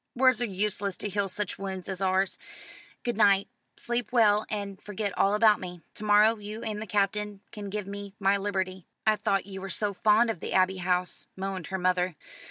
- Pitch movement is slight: Yes, narrow, 1.8 semitones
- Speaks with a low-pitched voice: No, high, 200 Hz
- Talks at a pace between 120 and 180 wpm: No, average, 200 wpm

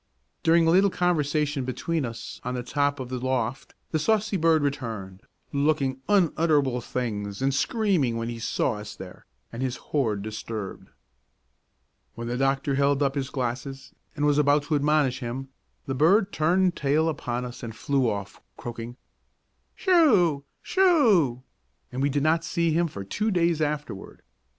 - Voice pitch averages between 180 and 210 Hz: No, medium, 140 Hz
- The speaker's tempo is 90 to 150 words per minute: No, average, 160 wpm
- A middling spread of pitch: Yes, average, 4.8 semitones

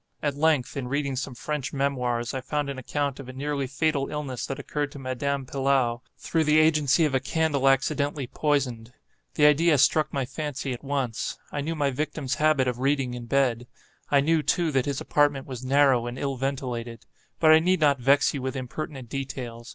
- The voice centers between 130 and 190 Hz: Yes, medium, 140 Hz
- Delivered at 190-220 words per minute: Yes, average, 200 wpm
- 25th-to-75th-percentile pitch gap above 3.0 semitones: No, narrow, 2.4 semitones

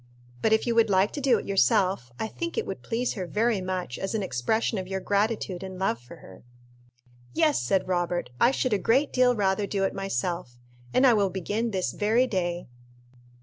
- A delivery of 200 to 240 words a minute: Yes, fast, 205 wpm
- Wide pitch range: No, average, 3.7 semitones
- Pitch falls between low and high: No, high, 195 Hz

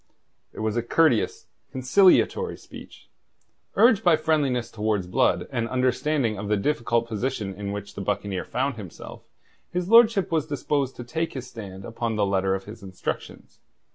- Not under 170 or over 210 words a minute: No, average, 160 wpm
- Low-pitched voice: Yes, low, 120 Hz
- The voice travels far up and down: Yes, wide, 6.6 semitones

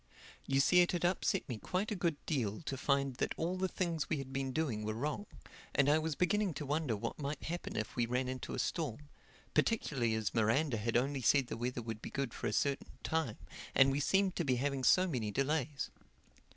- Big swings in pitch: No, average, 4.8 semitones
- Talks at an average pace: No, fast, 215 wpm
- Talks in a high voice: No, medium, 140 Hz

